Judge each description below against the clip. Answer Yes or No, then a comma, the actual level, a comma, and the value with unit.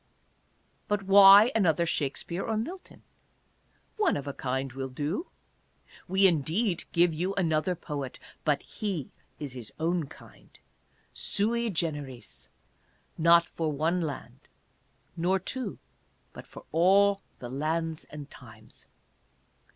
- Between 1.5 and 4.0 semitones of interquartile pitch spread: No, average, 5.1 semitones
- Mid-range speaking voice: Yes, medium, 165 Hz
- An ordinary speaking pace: No, slow, 130 wpm